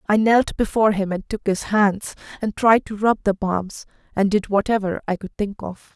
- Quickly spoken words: Yes, fast, 210 wpm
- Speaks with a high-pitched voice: Yes, high, 205 Hz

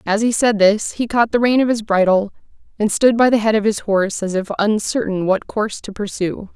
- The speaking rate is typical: No, fast, 240 wpm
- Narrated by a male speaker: No, female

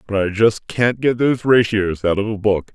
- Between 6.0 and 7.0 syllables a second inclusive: No, 5.0 syllables/s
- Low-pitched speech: Yes, low, 105 Hz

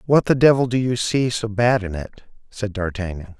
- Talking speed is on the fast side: Yes, fast, 210 wpm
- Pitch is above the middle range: No, low, 110 Hz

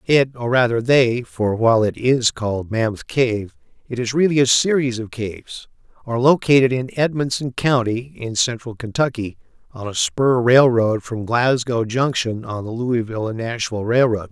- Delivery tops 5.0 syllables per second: No, 4.8 syllables/s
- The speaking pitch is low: Yes, low, 120 Hz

